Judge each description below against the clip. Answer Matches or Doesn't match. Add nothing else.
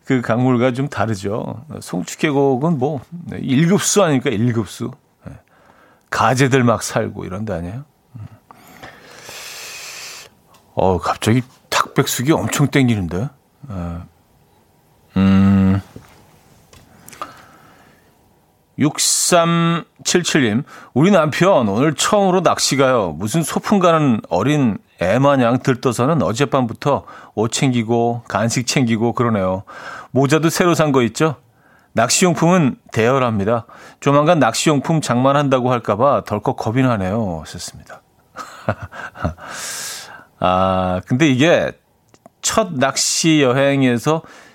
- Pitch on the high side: Doesn't match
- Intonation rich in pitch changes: Doesn't match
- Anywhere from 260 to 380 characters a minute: Doesn't match